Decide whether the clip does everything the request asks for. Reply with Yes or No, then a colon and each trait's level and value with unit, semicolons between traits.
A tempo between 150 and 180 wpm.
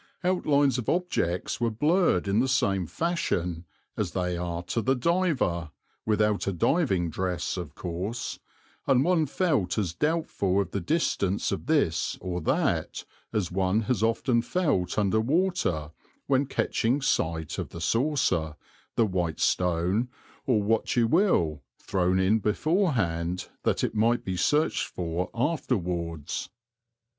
No: average, 140 wpm